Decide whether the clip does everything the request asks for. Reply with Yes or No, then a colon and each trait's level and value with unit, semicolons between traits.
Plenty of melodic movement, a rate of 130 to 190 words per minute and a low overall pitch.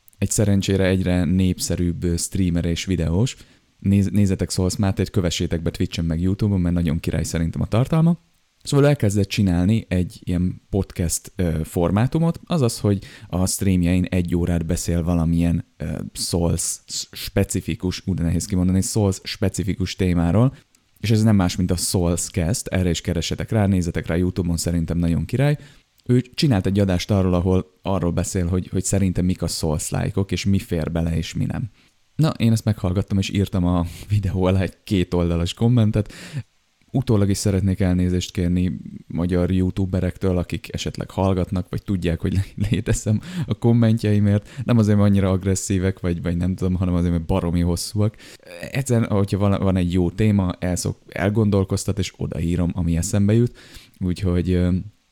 No: average, 2.9 semitones; average, 150 wpm; very low, 95 Hz